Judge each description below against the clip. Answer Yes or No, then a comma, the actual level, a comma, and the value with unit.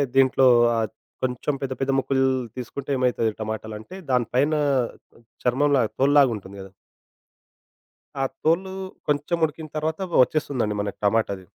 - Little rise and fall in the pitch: No, average, 4.7 semitones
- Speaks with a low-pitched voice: Yes, low, 130 Hz